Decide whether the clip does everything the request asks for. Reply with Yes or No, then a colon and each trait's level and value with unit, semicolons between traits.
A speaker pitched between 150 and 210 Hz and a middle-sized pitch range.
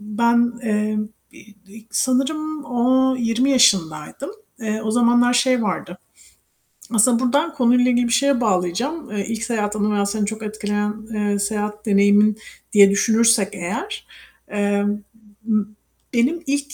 No: high, 225 Hz; average, 3.2 semitones